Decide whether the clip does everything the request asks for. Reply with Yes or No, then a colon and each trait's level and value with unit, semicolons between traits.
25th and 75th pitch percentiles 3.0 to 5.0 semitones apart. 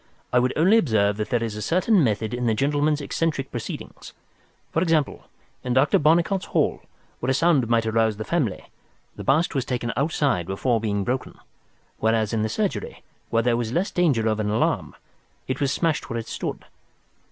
No: wide, 5.4 semitones